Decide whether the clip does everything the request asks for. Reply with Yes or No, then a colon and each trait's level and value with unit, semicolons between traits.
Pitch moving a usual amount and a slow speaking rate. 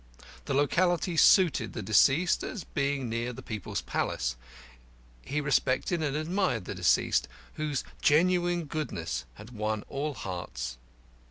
No: wide, 7.3 semitones; slow, 125 wpm